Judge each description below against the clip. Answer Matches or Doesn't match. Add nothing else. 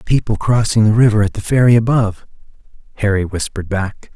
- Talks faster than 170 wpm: Doesn't match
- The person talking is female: Doesn't match